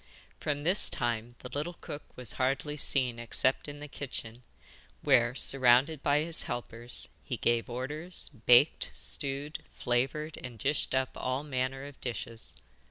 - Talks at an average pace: Yes, average, 145 wpm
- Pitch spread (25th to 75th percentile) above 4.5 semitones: No, average, 3.2 semitones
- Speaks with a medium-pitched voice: No, low, 130 Hz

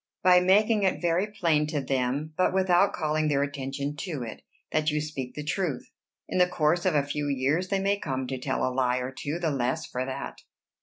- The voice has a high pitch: No, medium, 150 Hz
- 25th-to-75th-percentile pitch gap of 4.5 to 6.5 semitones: Yes, average, 4.9 semitones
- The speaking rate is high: Yes, fast, 215 wpm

